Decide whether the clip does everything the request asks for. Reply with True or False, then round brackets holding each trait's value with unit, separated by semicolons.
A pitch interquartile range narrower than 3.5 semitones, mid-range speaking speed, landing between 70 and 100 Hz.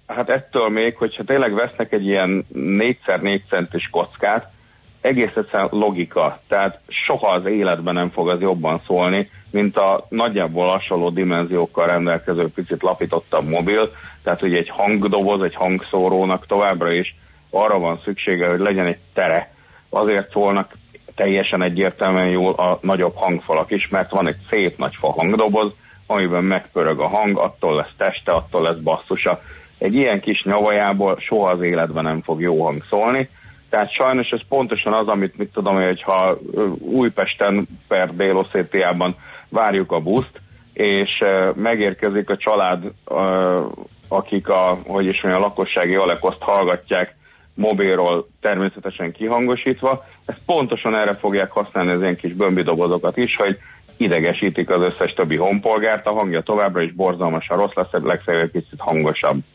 True (2.5 semitones; 145 wpm; 95 Hz)